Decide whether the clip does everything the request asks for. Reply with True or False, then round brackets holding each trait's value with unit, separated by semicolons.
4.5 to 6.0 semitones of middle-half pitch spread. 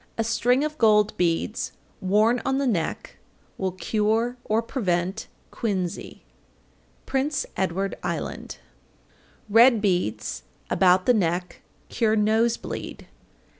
False (4.1 semitones)